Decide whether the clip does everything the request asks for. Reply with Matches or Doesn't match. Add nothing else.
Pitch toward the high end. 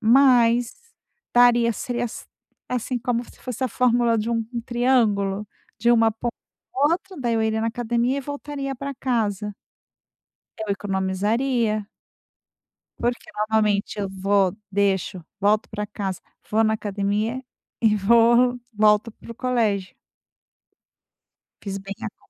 Matches